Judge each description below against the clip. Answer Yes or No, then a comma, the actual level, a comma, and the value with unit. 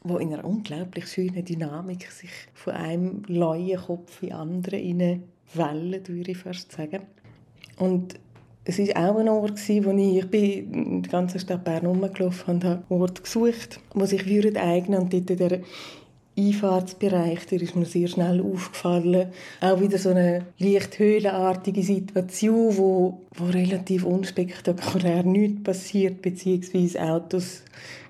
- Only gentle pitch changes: Yes, narrow, 1.5 semitones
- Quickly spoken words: No, average, 145 wpm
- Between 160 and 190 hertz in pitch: Yes, medium, 185 Hz